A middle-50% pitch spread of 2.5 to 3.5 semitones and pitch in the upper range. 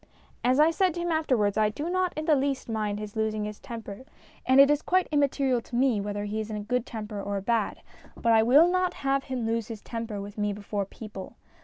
No: average, 4.8 semitones; high, 230 Hz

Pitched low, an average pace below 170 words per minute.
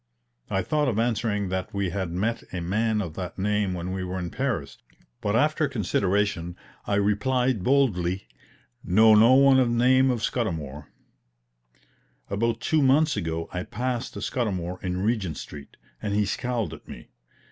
Yes: low, 105 Hz; average, 160 wpm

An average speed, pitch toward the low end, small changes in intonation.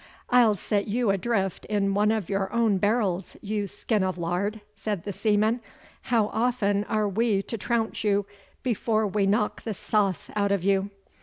No: average, 170 wpm; high, 205 Hz; narrow, 1.9 semitones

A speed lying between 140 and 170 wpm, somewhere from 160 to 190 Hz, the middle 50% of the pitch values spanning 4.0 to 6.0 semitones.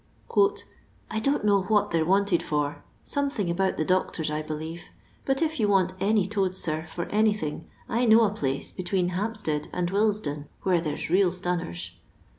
No: average, 180 wpm; medium, 185 Hz; average, 4.7 semitones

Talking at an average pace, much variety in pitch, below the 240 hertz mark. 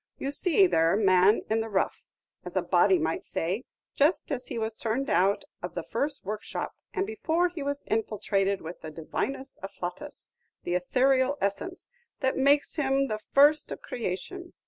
No: average, 170 wpm; wide, 6.7 semitones; very high, 260 Hz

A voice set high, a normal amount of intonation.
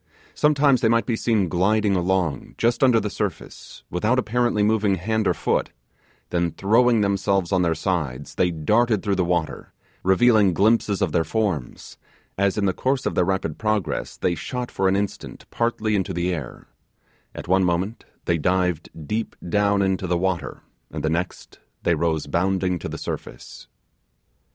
No: very low, 95 Hz; average, 3.8 semitones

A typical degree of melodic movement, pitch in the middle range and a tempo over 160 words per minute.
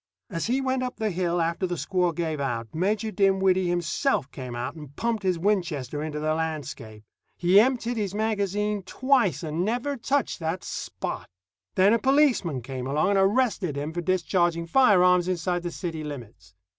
Yes: average, 5.0 semitones; medium, 180 Hz; average, 170 wpm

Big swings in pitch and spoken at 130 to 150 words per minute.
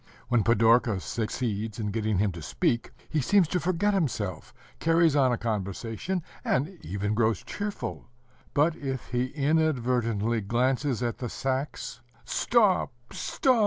Yes: wide, 5.9 semitones; slow, 135 wpm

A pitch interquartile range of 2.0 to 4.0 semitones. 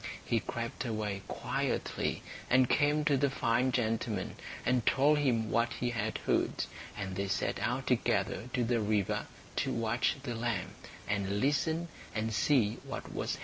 Yes: average, 3.1 semitones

